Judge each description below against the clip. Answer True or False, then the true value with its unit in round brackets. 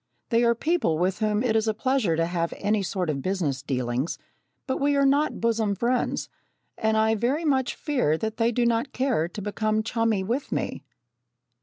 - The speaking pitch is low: False (220 Hz)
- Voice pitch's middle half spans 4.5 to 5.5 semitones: True (4.9 semitones)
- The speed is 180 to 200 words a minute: True (190 wpm)